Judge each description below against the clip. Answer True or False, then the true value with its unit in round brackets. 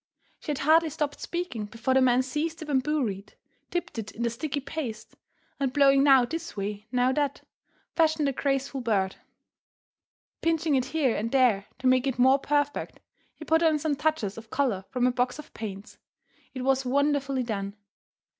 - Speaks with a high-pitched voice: True (265 Hz)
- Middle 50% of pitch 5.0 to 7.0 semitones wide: False (3.8 semitones)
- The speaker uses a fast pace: False (180 wpm)